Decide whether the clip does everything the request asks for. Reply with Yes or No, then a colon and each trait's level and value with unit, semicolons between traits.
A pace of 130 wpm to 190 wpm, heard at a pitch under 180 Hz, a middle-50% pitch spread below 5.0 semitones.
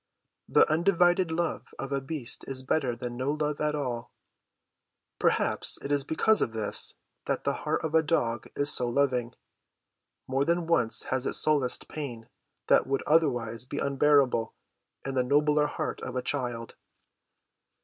Yes: average, 160 wpm; medium, 140 Hz; average, 3.5 semitones